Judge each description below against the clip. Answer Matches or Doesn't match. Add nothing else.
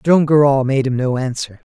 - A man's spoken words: Matches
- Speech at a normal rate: Doesn't match